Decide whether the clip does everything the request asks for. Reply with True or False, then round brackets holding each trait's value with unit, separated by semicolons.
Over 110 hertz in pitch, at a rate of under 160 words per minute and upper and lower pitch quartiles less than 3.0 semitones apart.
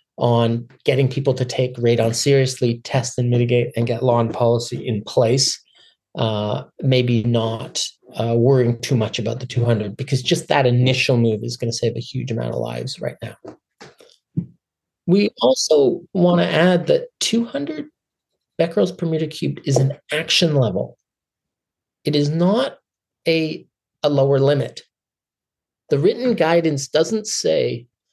False (135 Hz; 150 wpm; 5.5 semitones)